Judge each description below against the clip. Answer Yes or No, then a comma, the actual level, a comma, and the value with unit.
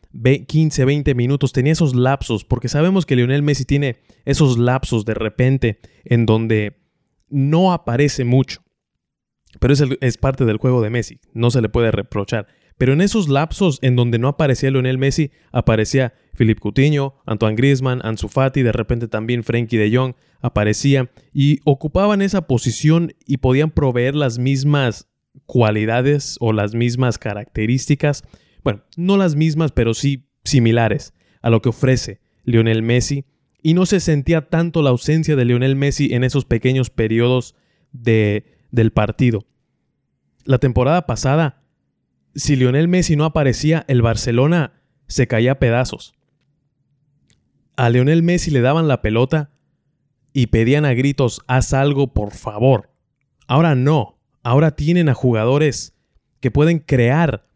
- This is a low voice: Yes, low, 130 Hz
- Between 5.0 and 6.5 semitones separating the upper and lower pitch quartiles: No, average, 3.4 semitones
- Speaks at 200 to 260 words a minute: No, average, 145 wpm